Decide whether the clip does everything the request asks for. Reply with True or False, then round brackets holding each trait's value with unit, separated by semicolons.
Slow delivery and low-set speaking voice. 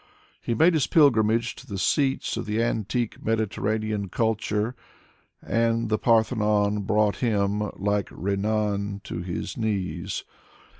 True (120 wpm; 110 Hz)